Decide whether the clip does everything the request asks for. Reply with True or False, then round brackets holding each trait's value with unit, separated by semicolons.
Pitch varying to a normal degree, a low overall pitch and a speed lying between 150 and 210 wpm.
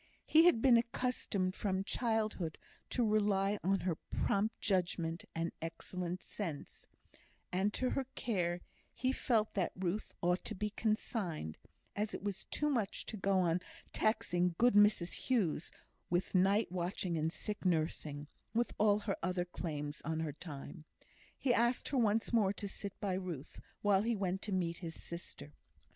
False (3.8 semitones; 190 Hz; 160 wpm)